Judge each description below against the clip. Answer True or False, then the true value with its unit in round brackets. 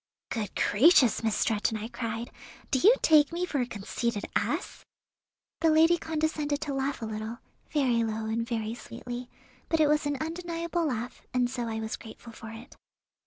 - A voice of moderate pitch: False (245 Hz)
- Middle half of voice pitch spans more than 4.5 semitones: True (5.6 semitones)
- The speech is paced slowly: False (175 wpm)